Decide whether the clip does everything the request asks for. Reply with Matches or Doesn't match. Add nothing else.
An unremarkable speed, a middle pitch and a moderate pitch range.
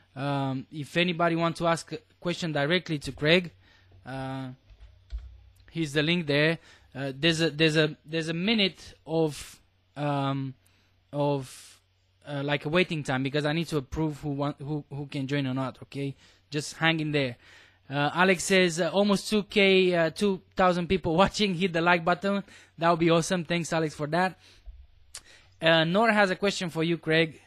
Matches